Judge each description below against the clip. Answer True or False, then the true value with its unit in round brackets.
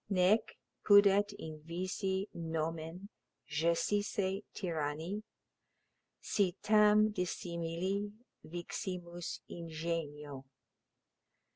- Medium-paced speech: False (55 wpm)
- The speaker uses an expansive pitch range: False (3.5 semitones)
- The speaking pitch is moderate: True (175 Hz)